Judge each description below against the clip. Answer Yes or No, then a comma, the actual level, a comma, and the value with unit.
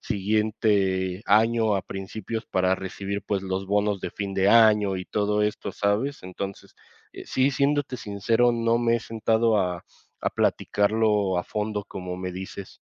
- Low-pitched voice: Yes, low, 105 Hz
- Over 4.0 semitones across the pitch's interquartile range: No, average, 2.7 semitones